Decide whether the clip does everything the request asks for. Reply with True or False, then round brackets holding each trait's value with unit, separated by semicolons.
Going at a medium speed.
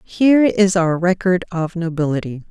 True (145 wpm)